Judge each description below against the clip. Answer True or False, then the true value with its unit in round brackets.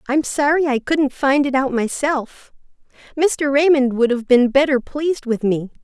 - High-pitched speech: True (270 Hz)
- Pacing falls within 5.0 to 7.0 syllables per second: False (4.5 syllables/s)